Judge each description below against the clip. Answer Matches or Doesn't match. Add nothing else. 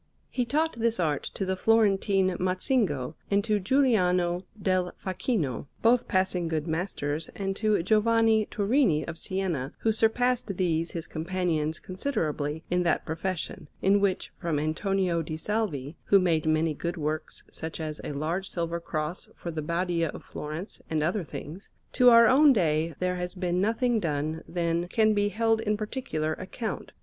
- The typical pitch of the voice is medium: Matches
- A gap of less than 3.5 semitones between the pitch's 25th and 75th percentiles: Doesn't match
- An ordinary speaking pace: Matches